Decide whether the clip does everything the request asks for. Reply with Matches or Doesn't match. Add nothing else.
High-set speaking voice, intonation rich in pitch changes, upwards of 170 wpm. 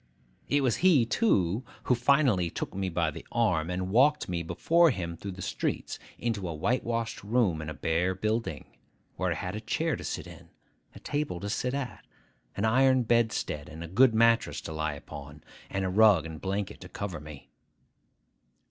Doesn't match